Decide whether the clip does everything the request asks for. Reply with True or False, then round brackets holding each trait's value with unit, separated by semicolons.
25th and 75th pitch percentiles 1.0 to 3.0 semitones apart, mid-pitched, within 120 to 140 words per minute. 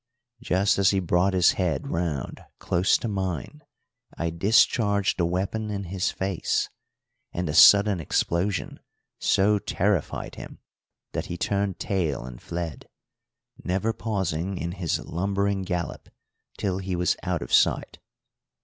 False (2.6 semitones; 95 Hz; 135 wpm)